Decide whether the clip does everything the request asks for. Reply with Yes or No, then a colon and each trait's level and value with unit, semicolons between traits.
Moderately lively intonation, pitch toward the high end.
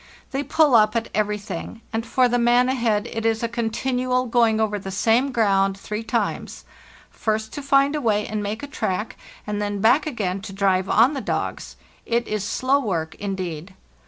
Yes: average, 3.4 semitones; high, 225 Hz